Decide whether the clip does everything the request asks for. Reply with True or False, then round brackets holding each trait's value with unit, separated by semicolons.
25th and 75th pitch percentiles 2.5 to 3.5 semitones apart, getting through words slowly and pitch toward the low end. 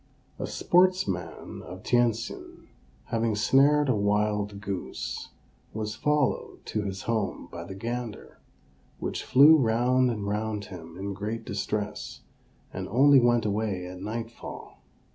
True (3.2 semitones; 125 wpm; 110 Hz)